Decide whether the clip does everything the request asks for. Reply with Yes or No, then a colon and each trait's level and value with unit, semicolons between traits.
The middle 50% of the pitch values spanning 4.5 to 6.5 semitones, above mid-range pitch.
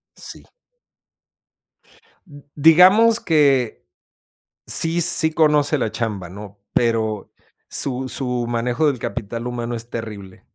No: average, 5.1 semitones; low, 125 Hz